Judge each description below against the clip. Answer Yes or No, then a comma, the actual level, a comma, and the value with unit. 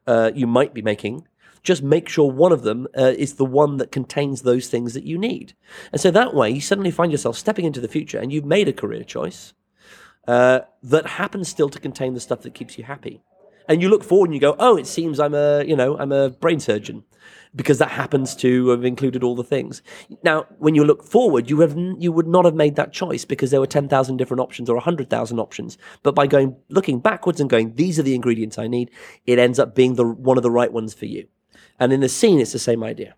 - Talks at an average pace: No, fast, 250 wpm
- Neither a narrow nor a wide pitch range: Yes, average, 4.4 semitones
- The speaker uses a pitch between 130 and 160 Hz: Yes, medium, 140 Hz